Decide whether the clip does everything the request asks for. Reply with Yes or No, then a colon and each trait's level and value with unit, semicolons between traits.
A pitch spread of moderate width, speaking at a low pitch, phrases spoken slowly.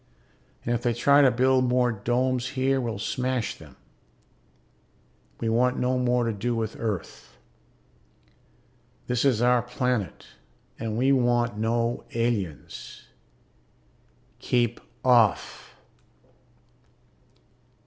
No: narrow, 1.7 semitones; low, 120 Hz; slow, 105 wpm